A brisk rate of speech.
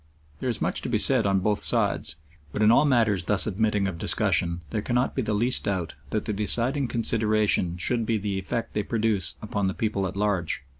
Yes: fast, 210 wpm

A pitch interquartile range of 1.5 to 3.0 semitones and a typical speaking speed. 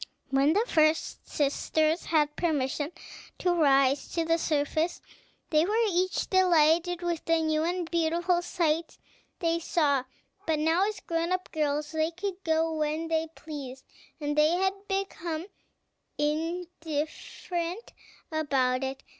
No: narrow, 2.5 semitones; slow, 130 wpm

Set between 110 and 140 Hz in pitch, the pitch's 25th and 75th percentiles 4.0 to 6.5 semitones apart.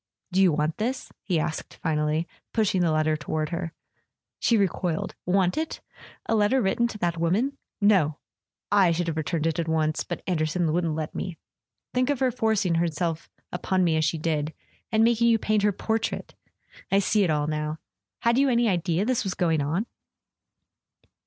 No: medium, 175 Hz; average, 5.2 semitones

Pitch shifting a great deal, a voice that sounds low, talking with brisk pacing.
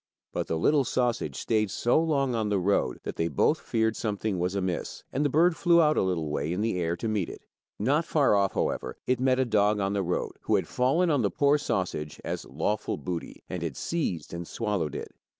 Yes: wide, 6.6 semitones; low, 105 Hz; fast, 225 wpm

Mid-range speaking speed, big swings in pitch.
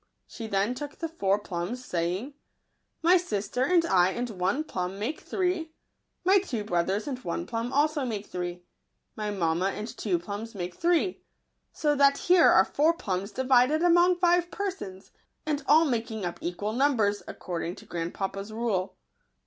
Yes: average, 165 wpm; wide, 8.1 semitones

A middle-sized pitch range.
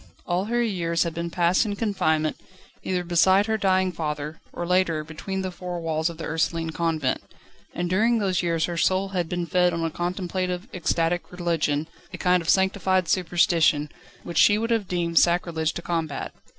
No: narrow, 2.3 semitones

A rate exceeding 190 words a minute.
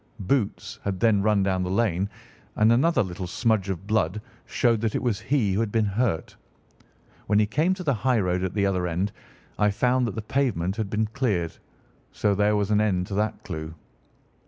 Yes: average, 200 wpm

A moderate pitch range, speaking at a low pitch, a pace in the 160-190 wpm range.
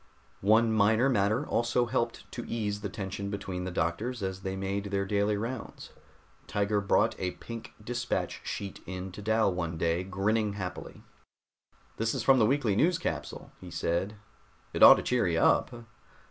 Yes: average, 3.2 semitones; low, 100 Hz; average, 170 wpm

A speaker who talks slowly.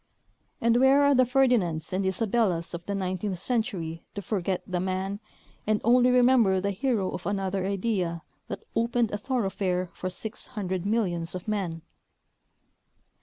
No: average, 150 wpm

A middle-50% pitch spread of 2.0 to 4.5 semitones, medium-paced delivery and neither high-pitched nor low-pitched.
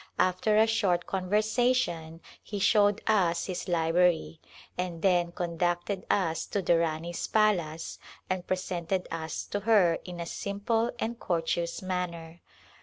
No: average, 3.2 semitones; slow, 130 wpm; medium, 180 Hz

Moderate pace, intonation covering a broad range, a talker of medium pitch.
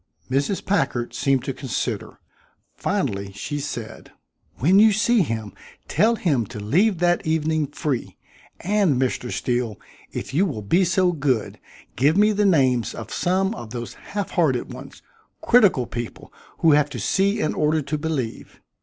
Yes: average, 155 wpm; wide, 7.2 semitones; medium, 150 Hz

